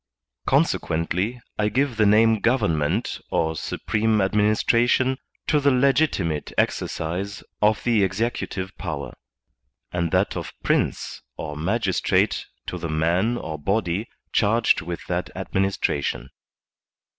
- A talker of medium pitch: No, low, 100 Hz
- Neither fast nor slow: No, slow, 110 wpm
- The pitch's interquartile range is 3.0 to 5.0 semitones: No, wide, 5.4 semitones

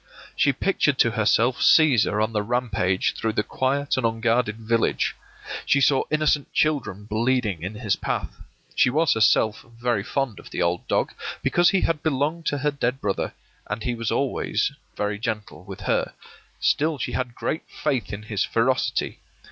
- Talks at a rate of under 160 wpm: No, average, 170 wpm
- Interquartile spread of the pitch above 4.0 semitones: Yes, average, 4.6 semitones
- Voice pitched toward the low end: Yes, low, 120 Hz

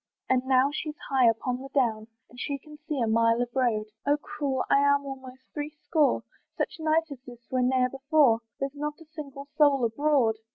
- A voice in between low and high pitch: No, very high, 270 Hz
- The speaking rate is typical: Yes, average, 195 wpm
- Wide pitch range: No, average, 3.0 semitones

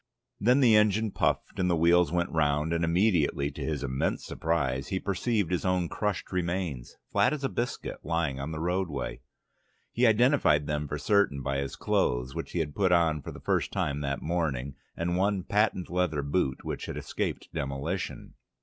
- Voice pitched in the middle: No, very low, 85 Hz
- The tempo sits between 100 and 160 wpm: No, average, 185 wpm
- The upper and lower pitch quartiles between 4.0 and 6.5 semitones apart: Yes, average, 4.9 semitones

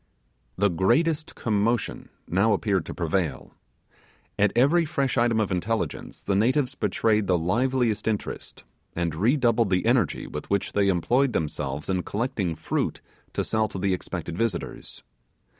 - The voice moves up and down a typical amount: Yes, average, 4.6 semitones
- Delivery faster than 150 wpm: No, average, 140 wpm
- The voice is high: No, low, 105 Hz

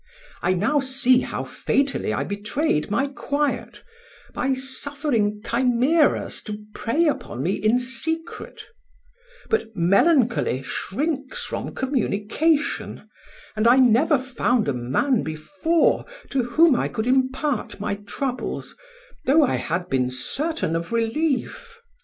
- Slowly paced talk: Yes, slow, 120 wpm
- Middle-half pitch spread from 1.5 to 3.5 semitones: No, wide, 5.6 semitones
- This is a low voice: No, very high, 255 Hz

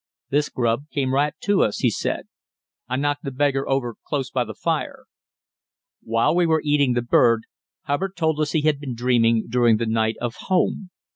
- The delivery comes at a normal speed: Yes, average, 190 wpm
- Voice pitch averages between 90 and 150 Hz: Yes, low, 135 Hz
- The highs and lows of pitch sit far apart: No, average, 3.9 semitones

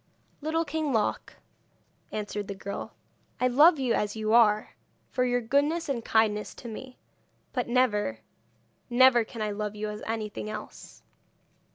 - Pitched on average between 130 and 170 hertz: No, high, 230 Hz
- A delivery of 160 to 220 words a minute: No, average, 150 wpm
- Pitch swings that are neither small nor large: Yes, average, 3.5 semitones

